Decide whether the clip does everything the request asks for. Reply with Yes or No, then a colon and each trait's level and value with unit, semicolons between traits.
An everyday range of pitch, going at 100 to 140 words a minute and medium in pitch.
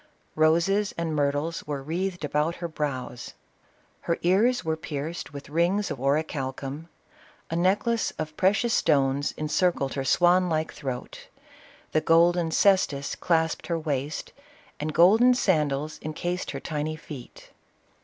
Yes: average, 3.3 semitones; slow, 135 wpm; medium, 160 Hz